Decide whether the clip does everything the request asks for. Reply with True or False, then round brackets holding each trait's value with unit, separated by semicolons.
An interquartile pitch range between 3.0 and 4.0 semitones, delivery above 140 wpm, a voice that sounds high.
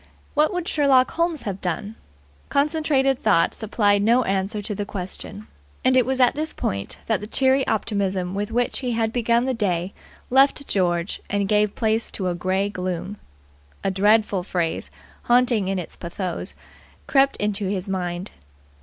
False (5.0 semitones; 165 wpm; 210 Hz)